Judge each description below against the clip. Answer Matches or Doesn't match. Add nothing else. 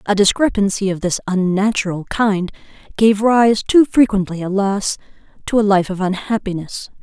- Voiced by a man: Doesn't match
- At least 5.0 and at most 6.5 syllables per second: Doesn't match